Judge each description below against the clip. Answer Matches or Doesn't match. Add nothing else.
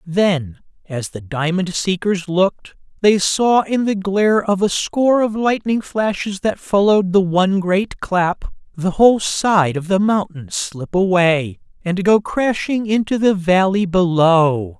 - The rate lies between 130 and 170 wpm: Matches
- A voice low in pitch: Doesn't match